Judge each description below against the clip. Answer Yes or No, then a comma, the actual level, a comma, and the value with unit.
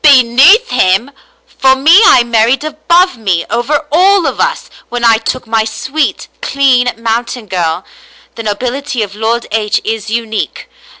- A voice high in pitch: Yes, high, 240 Hz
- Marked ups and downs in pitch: No, average, 4.2 semitones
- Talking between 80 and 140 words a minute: No, average, 155 wpm